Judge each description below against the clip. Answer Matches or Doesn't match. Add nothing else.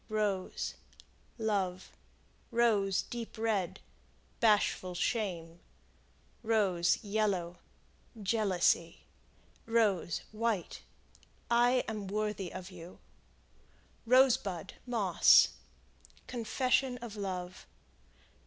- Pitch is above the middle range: Matches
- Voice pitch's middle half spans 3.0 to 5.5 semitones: Matches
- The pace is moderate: Doesn't match